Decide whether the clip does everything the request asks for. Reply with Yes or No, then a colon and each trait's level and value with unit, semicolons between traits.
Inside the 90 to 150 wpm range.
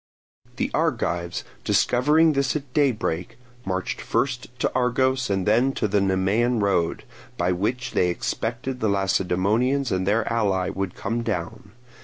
Yes: average, 140 wpm